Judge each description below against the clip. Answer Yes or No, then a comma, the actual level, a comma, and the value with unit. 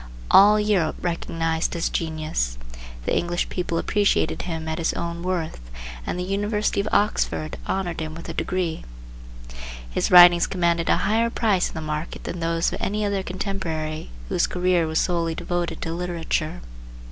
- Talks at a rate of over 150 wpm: Yes, average, 160 wpm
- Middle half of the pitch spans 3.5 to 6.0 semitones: No, narrow, 2.6 semitones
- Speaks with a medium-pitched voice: Yes, medium, 175 Hz